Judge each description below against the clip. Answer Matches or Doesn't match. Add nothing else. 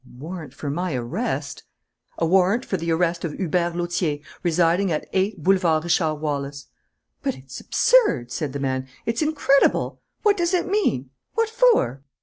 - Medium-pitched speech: Matches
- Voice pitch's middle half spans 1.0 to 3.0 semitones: Doesn't match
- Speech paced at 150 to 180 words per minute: Matches